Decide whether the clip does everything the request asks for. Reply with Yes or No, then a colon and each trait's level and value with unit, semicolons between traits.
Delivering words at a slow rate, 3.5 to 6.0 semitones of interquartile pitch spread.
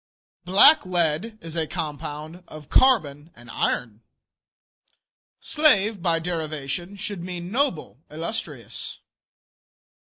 Yes: slow, 90 wpm; average, 4.3 semitones